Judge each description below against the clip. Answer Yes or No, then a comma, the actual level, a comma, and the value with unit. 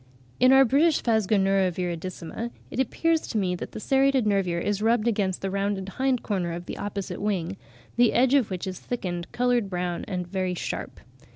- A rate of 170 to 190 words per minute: Yes, average, 185 wpm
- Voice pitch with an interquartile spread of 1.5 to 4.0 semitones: No, average, 4.8 semitones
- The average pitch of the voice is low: No, high, 200 Hz